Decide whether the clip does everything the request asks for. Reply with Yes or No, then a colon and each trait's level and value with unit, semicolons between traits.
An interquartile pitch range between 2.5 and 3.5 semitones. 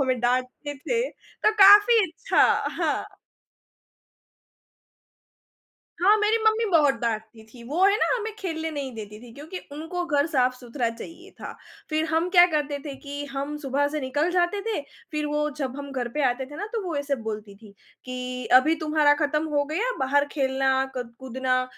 No: average, 4.4 semitones